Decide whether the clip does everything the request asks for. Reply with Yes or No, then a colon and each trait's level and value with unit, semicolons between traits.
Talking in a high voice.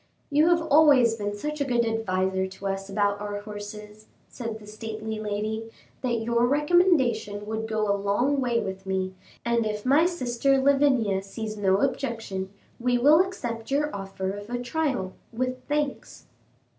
Yes: high, 225 Hz